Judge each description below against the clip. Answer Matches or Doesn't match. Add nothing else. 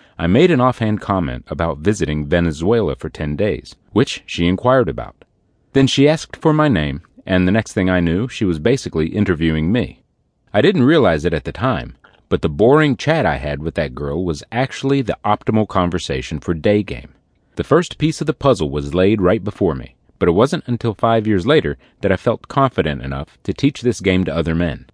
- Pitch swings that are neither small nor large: Doesn't match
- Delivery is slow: Doesn't match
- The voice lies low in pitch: Matches